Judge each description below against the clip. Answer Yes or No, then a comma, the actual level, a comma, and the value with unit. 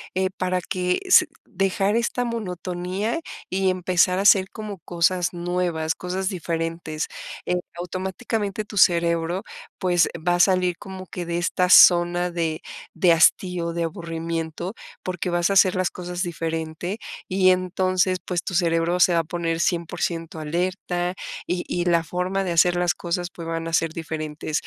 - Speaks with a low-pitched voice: No, medium, 175 Hz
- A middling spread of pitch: No, narrow, 1.6 semitones